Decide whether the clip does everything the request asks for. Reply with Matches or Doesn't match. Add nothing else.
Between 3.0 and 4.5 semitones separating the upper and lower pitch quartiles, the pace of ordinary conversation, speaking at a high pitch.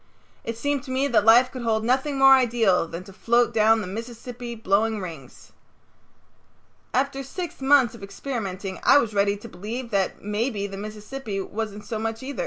Matches